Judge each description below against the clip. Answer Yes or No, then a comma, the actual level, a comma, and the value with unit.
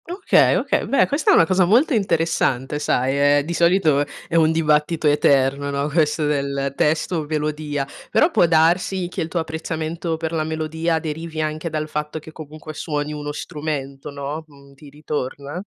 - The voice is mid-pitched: Yes, medium, 155 Hz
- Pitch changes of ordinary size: No, narrow, 2.0 semitones